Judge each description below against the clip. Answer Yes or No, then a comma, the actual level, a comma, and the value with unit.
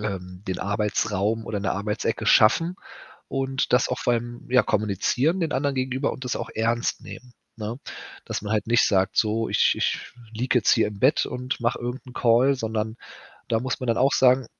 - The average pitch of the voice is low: Yes, low, 115 Hz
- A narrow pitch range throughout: No, average, 3.2 semitones